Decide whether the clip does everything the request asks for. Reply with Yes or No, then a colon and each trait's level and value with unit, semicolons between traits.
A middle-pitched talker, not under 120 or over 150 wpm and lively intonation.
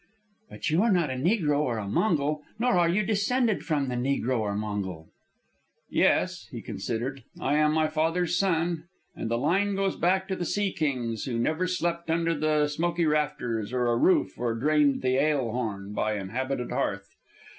No: medium, 150 Hz; average, 180 wpm; wide, 6.0 semitones